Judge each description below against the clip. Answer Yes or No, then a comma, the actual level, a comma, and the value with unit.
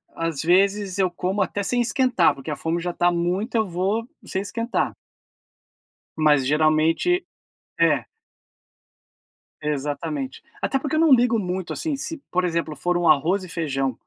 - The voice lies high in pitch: No, medium, 180 Hz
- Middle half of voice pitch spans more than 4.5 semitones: Yes, average, 5.1 semitones